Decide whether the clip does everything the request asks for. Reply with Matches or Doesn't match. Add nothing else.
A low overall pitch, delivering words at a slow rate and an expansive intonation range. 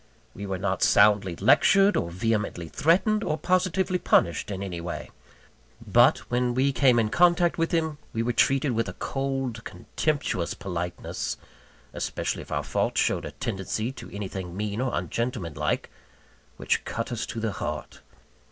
Doesn't match